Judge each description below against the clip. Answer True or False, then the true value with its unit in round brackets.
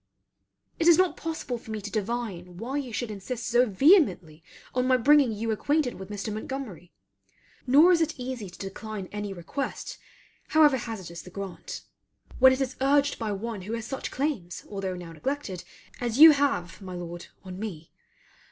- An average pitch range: False (5.9 semitones)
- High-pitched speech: True (225 Hz)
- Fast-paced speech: False (175 wpm)